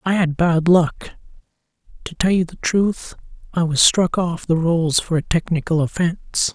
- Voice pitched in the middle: Yes, medium, 170 Hz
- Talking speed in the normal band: Yes, average, 165 wpm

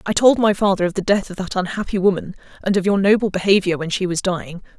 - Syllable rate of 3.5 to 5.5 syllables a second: No, 6.6 syllables/s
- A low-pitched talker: No, high, 190 Hz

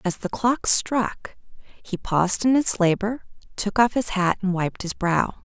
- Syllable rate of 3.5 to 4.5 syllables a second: Yes, 4.1 syllables/s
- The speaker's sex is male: No, female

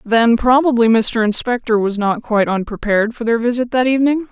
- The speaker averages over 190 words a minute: No, average, 180 wpm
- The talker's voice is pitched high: Yes, high, 230 Hz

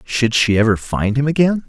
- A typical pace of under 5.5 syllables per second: Yes, 5.1 syllables/s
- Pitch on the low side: Yes, low, 125 Hz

